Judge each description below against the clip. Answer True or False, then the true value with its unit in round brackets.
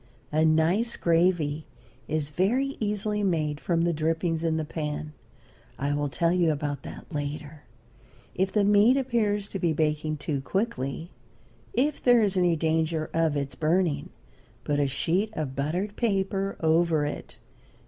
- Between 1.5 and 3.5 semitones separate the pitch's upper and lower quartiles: False (4.4 semitones)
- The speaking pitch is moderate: True (165 Hz)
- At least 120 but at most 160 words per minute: True (150 wpm)